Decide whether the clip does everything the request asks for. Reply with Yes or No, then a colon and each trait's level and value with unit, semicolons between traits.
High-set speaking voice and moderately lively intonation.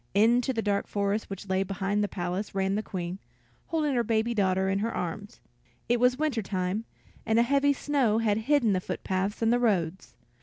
Yes: high, 210 Hz; average, 3.6 semitones